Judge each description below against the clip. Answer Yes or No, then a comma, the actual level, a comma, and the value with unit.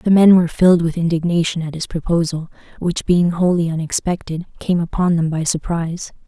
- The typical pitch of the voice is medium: Yes, medium, 170 Hz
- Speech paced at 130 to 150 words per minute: No, average, 170 wpm